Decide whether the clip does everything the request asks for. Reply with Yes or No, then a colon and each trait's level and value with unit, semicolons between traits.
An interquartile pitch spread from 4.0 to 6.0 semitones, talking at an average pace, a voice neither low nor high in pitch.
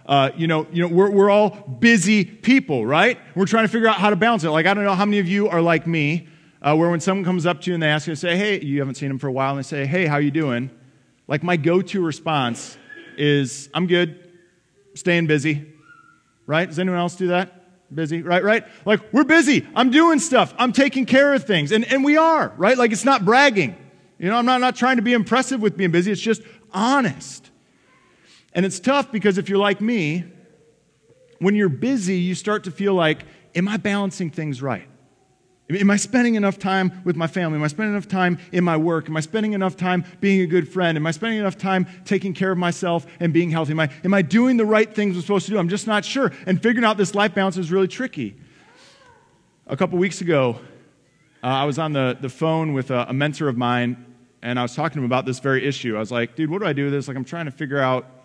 No: average, 5.2 semitones; fast, 245 wpm; medium, 180 Hz